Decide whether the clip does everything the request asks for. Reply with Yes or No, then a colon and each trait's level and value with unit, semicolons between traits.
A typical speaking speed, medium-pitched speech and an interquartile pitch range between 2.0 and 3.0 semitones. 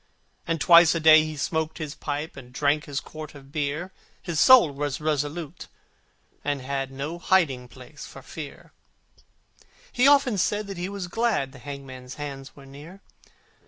No: average, 160 wpm; medium, 150 Hz; average, 3.8 semitones